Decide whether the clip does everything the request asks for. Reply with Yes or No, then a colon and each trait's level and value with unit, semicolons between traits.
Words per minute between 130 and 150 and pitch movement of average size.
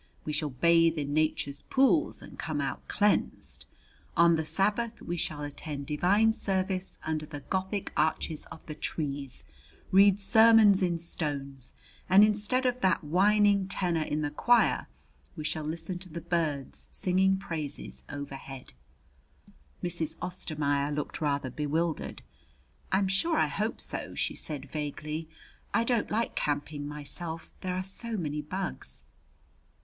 Yes: average, 140 wpm; average, 4.6 semitones